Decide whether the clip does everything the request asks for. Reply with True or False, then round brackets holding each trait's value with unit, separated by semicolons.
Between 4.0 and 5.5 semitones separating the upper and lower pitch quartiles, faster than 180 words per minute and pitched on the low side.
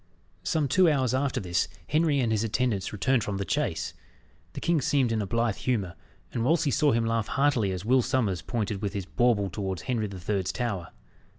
True (4.8 semitones; 200 wpm; 115 Hz)